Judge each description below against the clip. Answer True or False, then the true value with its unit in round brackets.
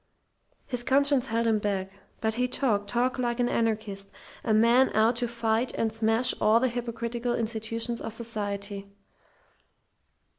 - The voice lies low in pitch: False (230 Hz)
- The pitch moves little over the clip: True (1.8 semitones)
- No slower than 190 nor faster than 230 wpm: False (145 wpm)